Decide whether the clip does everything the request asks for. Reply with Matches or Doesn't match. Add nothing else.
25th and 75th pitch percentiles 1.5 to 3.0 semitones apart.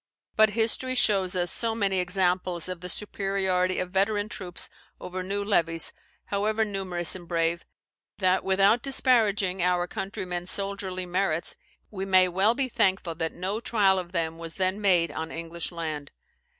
Matches